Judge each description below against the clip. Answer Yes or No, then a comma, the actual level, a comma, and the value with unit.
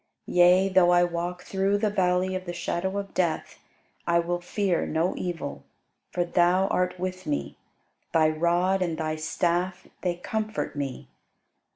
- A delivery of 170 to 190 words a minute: No, average, 155 wpm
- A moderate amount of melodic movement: No, narrow, 1.5 semitones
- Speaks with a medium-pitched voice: Yes, medium, 175 Hz